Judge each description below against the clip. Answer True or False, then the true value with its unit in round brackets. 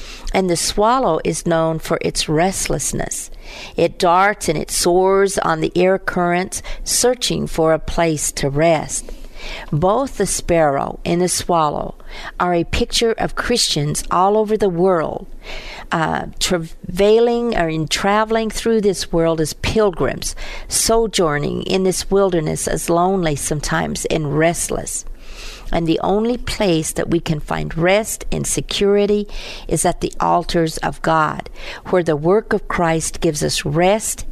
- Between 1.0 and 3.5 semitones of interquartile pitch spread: False (4.1 semitones)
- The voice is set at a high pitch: False (180 Hz)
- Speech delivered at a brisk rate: False (145 wpm)